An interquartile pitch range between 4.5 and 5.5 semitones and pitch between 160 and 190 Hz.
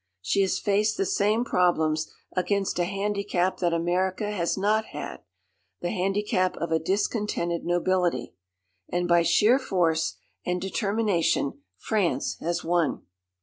No: average, 3.0 semitones; medium, 185 Hz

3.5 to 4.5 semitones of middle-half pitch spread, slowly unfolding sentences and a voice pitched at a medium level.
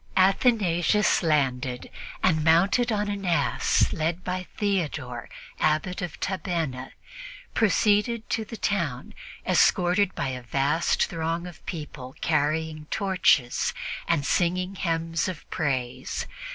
Yes: average, 4.2 semitones; slow, 110 wpm; medium, 170 Hz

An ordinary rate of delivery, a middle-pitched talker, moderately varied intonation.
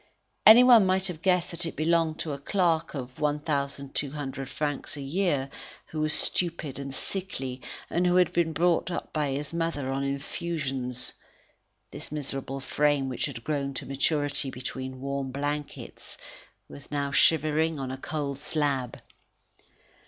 Yes: average, 145 wpm; medium, 145 Hz; average, 3.2 semitones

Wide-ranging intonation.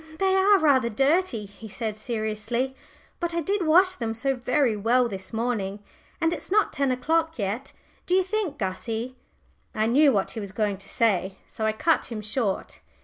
Yes: wide, 6.8 semitones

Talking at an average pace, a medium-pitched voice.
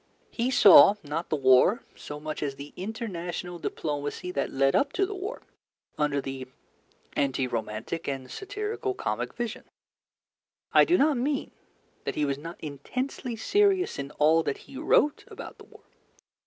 Yes: average, 155 wpm; medium, 170 Hz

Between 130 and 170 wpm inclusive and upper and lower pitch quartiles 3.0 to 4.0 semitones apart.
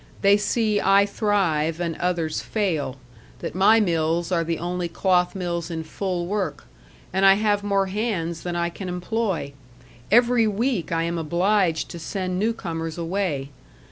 Yes: average, 160 wpm; average, 3.4 semitones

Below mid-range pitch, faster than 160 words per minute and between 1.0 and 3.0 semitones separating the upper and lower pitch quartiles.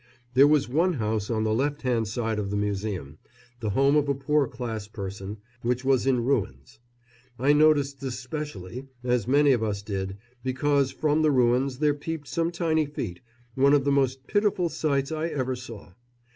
No: low, 130 Hz; average, 185 wpm; average, 4.9 semitones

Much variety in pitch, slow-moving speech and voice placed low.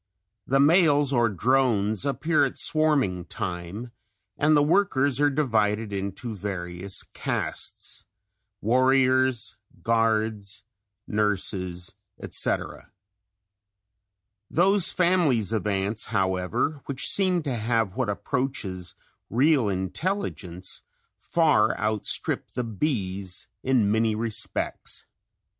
Yes: wide, 5.8 semitones; slow, 95 wpm; low, 115 Hz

